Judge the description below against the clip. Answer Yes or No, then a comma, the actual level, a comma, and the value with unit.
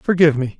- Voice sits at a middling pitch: Yes, medium, 155 Hz